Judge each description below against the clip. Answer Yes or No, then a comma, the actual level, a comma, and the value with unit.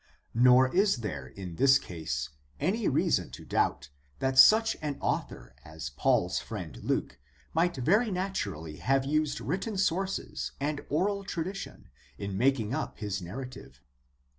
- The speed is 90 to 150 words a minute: Yes, average, 140 wpm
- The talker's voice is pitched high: No, low, 135 Hz